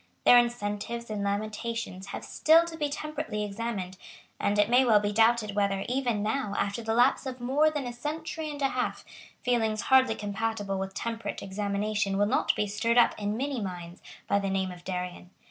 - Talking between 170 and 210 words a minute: Yes, average, 190 wpm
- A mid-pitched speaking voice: No, high, 220 Hz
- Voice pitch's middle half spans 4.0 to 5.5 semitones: No, average, 3.5 semitones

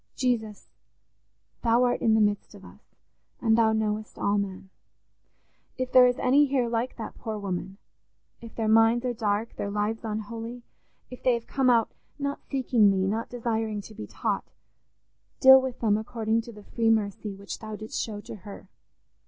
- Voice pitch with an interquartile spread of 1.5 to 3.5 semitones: Yes, narrow, 2.5 semitones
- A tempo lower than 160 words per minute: No, average, 170 wpm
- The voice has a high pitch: Yes, high, 225 Hz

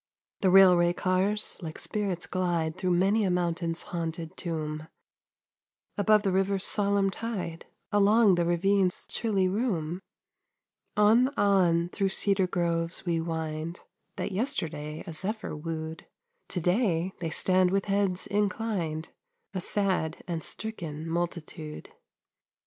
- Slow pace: Yes, slow, 120 wpm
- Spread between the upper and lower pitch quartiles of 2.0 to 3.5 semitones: Yes, average, 3.2 semitones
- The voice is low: No, medium, 180 Hz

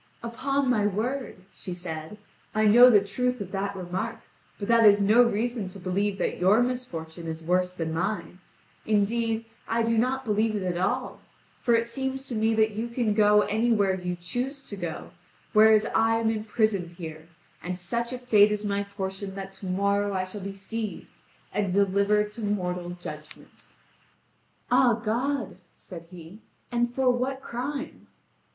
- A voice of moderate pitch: No, high, 210 Hz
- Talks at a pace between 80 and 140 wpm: No, average, 170 wpm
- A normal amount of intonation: Yes, average, 3.9 semitones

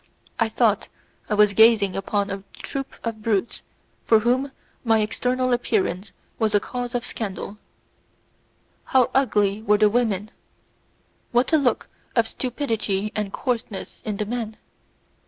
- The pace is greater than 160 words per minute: No, slow, 135 wpm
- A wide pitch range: No, average, 3.0 semitones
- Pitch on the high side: Yes, high, 220 Hz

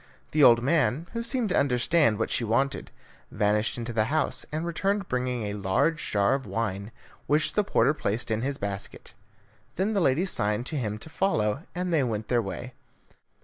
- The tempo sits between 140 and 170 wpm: No, average, 190 wpm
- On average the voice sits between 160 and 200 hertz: No, low, 125 Hz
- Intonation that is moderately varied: No, wide, 6.9 semitones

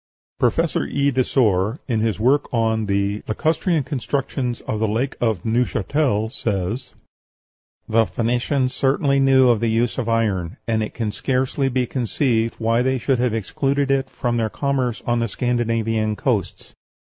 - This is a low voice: Yes, low, 120 Hz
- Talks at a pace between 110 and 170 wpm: Yes, average, 150 wpm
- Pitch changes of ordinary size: Yes, average, 3.1 semitones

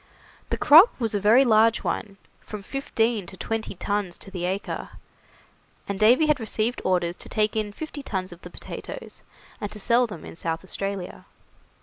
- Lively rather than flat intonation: No, average, 3.3 semitones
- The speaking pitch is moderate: No, high, 210 Hz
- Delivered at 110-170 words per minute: No, average, 180 wpm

